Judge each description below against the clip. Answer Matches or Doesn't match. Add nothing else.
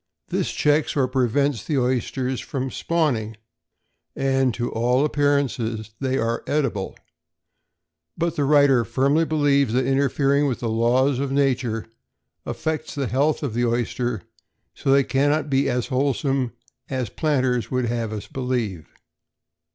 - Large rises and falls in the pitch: Doesn't match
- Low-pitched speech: Matches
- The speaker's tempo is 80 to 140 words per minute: Matches